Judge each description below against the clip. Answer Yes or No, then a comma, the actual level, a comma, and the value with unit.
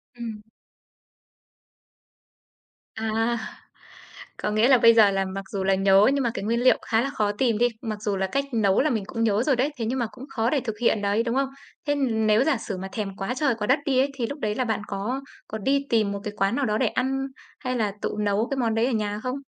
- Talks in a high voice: Yes, high, 225 Hz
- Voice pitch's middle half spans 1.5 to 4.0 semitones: Yes, average, 3.6 semitones